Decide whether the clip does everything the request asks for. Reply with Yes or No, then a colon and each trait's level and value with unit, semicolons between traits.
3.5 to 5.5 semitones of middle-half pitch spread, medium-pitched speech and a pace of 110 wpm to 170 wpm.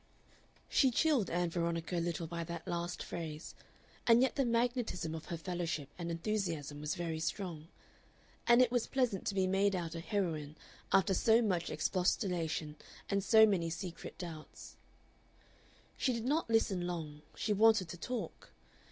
Yes: average, 4.8 semitones; medium, 180 Hz; average, 160 wpm